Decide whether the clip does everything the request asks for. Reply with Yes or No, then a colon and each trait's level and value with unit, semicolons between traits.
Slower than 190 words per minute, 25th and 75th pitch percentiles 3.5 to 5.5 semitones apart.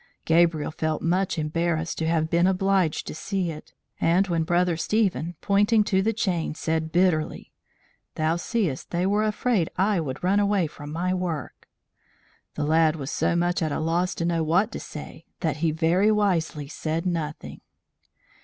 No: average, 170 wpm; average, 3.0 semitones